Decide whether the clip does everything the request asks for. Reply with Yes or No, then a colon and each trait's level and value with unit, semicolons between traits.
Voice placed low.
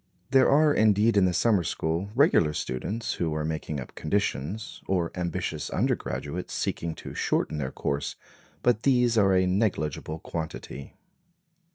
Yes: very low, 90 Hz